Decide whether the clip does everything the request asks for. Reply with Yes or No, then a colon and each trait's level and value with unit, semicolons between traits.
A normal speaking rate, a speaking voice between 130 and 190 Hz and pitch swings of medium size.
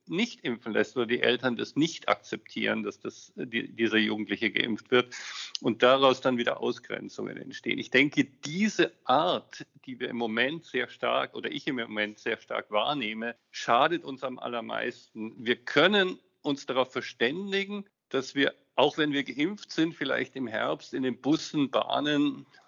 Yes: average, 165 wpm; low, 135 Hz; average, 4.9 semitones